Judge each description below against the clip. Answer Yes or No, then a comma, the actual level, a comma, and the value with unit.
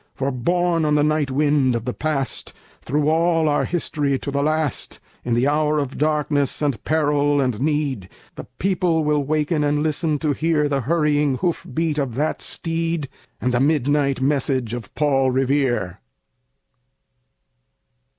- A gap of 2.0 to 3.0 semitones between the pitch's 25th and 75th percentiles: Yes, narrow, 2.5 semitones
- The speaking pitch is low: No, medium, 145 Hz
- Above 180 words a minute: No, average, 155 wpm